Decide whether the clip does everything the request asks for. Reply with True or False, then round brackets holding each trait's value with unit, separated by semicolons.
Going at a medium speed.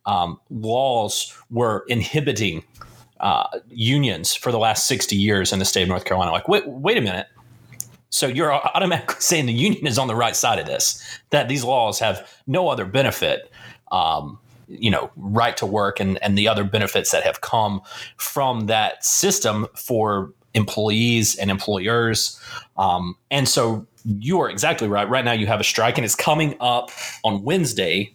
True (175 wpm)